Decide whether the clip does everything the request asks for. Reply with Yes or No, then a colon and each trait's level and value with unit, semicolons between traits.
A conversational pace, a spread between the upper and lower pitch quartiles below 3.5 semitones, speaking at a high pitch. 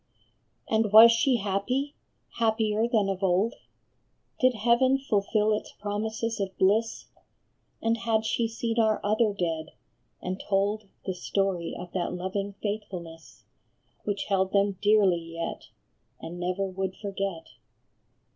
No: slow, 125 wpm; average, 2.9 semitones; high, 205 Hz